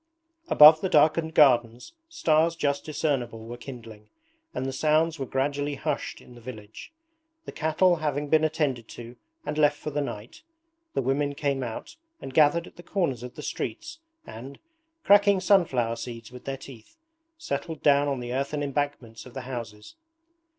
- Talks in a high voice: No, medium, 140 Hz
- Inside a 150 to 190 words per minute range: Yes, average, 165 wpm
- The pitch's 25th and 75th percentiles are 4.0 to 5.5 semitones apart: Yes, average, 4.3 semitones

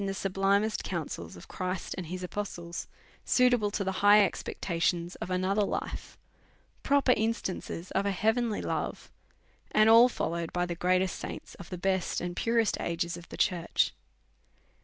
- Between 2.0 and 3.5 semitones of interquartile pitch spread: Yes, average, 3.2 semitones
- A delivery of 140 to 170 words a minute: Yes, average, 165 wpm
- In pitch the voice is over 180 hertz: Yes, high, 190 Hz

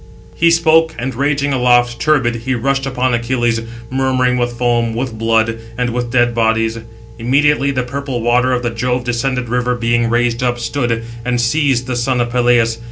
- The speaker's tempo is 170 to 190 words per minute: Yes, average, 175 wpm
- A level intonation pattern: Yes, narrow, 1.8 semitones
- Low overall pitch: Yes, low, 125 Hz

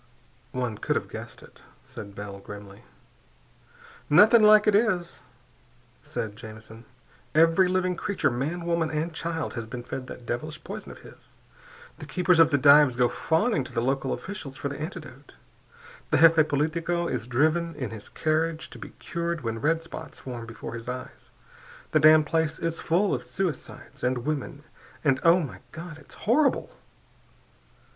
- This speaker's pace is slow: No, average, 165 wpm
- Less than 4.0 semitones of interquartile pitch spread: No, average, 5.0 semitones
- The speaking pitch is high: No, medium, 155 Hz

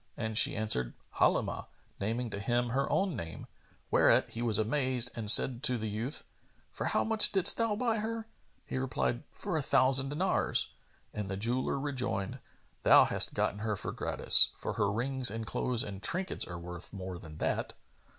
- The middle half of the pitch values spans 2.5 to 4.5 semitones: No, average, 5.0 semitones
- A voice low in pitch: Yes, low, 115 Hz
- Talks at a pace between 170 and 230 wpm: Yes, average, 175 wpm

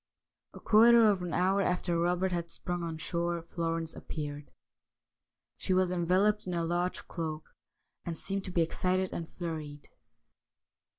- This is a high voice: No, medium, 175 Hz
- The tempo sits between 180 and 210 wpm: No, average, 145 wpm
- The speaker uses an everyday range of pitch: No, narrow, 2.0 semitones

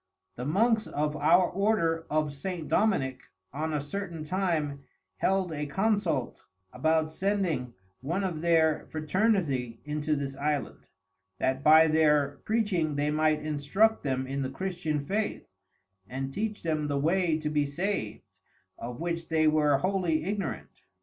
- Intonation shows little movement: No, average, 4.2 semitones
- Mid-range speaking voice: Yes, medium, 155 Hz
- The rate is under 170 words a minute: Yes, average, 145 wpm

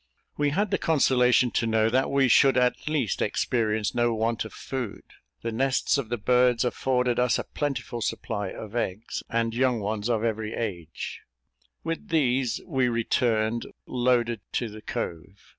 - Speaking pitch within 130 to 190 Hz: No, low, 120 Hz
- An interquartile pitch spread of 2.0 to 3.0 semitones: Yes, narrow, 2.6 semitones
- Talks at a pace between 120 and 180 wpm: Yes, average, 160 wpm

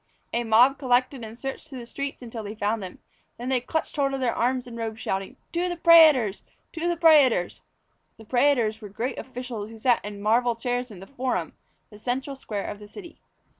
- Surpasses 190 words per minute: Yes, fast, 205 wpm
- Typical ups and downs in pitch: Yes, average, 3.6 semitones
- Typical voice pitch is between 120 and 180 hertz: No, high, 245 Hz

